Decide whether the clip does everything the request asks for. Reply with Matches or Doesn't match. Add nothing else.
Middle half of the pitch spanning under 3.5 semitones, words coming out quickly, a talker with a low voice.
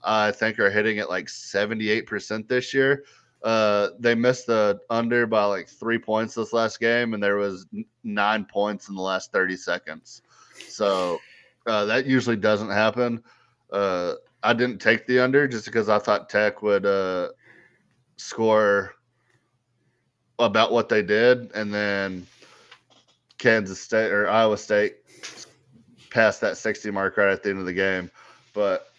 Doesn't match